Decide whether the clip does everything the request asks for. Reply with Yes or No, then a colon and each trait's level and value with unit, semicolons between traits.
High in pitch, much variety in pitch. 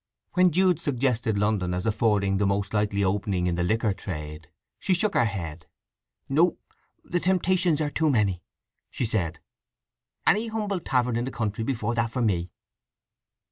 No: low, 110 Hz; wide, 7.3 semitones